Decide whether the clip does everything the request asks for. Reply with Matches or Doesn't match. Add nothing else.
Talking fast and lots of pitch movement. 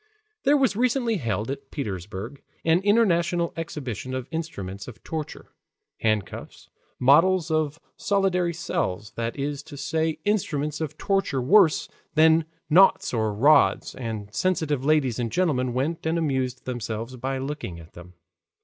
Doesn't match